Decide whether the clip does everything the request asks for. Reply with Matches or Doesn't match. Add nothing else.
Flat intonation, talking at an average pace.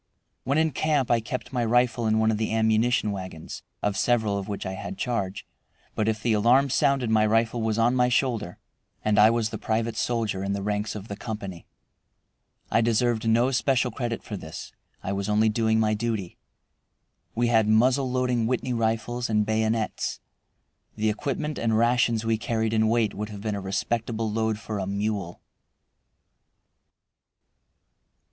Matches